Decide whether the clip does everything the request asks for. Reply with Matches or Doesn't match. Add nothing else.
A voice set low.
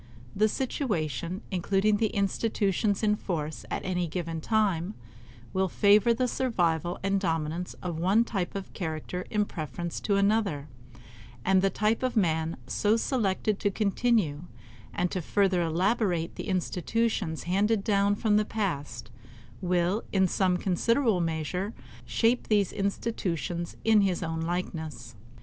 Doesn't match